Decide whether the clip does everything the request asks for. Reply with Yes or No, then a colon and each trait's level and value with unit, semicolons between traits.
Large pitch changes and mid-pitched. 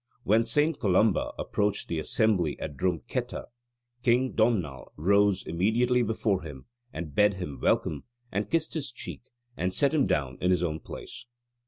No: wide, 5.7 semitones; low, 100 Hz